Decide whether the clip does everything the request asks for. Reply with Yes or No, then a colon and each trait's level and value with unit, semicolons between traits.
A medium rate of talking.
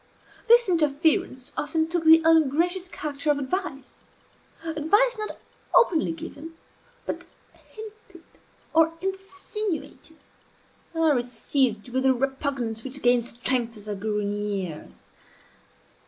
No: slow, 115 wpm